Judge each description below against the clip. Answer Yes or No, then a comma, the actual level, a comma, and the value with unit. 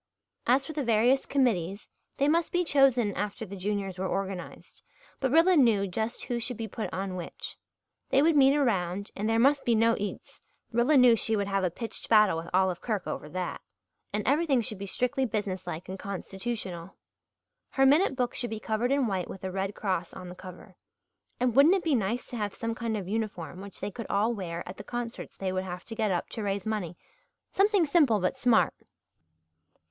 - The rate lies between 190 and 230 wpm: Yes, fast, 205 wpm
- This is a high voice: Yes, high, 215 Hz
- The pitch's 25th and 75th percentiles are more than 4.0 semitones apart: Yes, average, 4.7 semitones